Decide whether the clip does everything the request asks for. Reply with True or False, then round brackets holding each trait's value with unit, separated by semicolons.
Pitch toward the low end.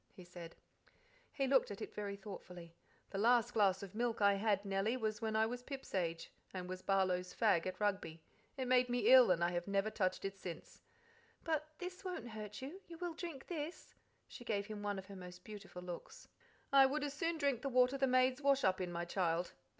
False (210 Hz)